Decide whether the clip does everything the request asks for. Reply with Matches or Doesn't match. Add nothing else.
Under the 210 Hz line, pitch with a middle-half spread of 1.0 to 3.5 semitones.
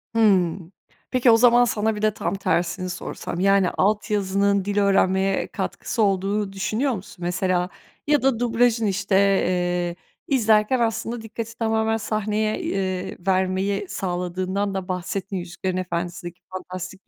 Matches